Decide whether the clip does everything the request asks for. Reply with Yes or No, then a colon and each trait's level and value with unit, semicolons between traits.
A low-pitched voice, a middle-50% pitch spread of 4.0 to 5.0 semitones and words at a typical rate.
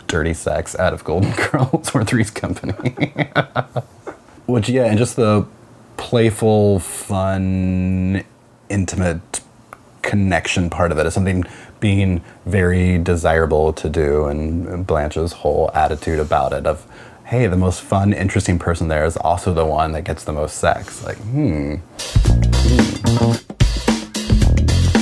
No: very low, 95 Hz; average, 4.7 semitones; slow, 130 wpm